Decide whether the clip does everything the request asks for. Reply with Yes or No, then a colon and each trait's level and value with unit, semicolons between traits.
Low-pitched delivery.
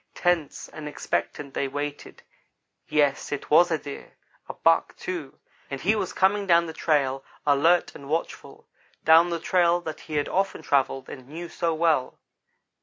No: medium, 155 Hz